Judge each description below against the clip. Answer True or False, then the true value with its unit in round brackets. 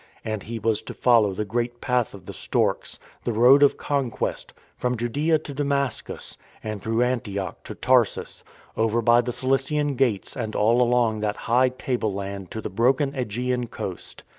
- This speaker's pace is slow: False (165 wpm)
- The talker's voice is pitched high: False (120 Hz)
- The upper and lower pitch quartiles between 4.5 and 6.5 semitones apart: False (2.9 semitones)